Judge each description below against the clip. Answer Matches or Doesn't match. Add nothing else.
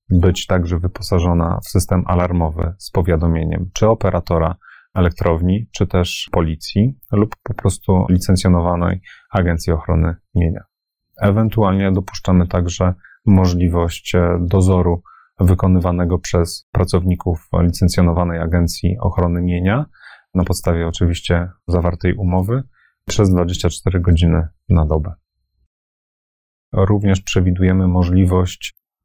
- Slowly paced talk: Matches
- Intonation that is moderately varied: Doesn't match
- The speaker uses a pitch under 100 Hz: Matches